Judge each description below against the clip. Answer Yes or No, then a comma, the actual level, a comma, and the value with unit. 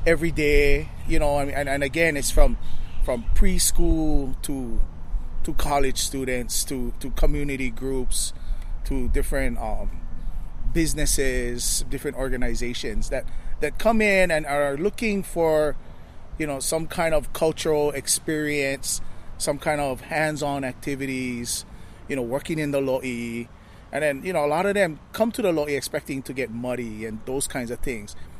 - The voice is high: No, low, 135 Hz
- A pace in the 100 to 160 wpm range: Yes, average, 150 wpm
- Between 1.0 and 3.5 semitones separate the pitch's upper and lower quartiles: No, average, 4.1 semitones